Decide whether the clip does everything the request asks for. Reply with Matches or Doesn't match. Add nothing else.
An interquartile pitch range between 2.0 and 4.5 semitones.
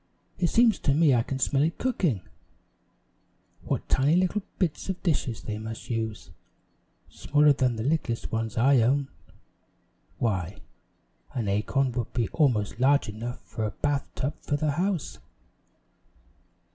Doesn't match